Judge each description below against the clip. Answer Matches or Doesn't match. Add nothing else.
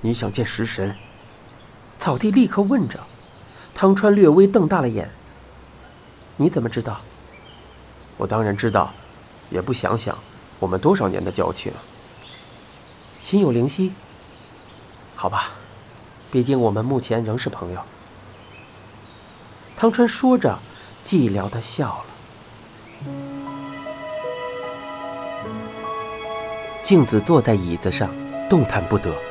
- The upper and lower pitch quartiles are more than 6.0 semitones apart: Matches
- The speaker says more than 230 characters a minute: Doesn't match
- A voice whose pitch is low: Matches